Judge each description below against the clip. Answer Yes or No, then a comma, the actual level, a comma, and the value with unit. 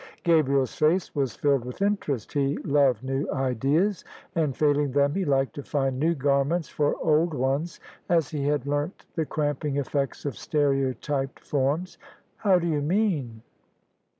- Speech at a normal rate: Yes, average, 155 wpm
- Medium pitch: Yes, medium, 145 Hz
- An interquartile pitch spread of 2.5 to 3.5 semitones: Yes, average, 2.8 semitones